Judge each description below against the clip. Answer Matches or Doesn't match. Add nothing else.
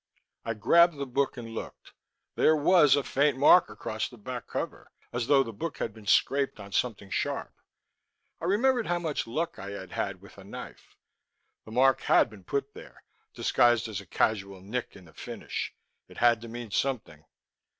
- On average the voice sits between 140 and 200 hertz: Doesn't match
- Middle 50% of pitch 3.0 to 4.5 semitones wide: Doesn't match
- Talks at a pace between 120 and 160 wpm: Doesn't match